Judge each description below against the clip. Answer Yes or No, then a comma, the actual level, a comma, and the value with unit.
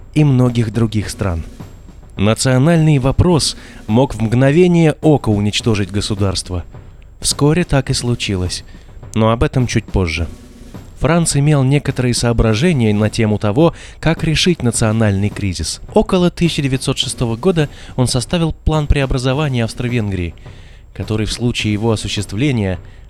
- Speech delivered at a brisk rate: No, average, 115 wpm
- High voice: No, low, 120 Hz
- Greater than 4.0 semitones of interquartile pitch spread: Yes, average, 5.1 semitones